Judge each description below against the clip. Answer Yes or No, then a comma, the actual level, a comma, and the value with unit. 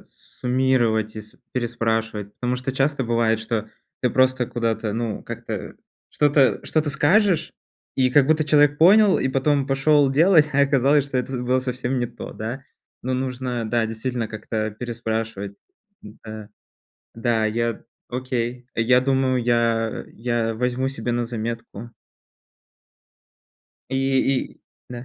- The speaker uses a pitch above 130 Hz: No, low, 125 Hz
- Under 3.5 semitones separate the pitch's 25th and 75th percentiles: Yes, average, 2.8 semitones